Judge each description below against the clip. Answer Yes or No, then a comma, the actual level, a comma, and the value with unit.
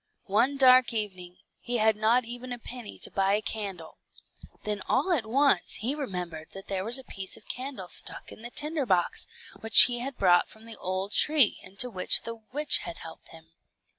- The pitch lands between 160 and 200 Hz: No, high, 220 Hz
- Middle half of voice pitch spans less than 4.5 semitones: No, average, 4.8 semitones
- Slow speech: No, average, 195 wpm